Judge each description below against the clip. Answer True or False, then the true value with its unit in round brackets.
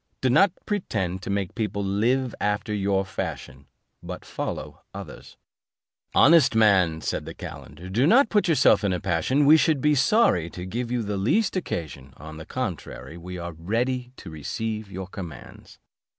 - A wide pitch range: True (6.3 semitones)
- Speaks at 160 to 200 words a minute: True (165 wpm)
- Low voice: True (105 Hz)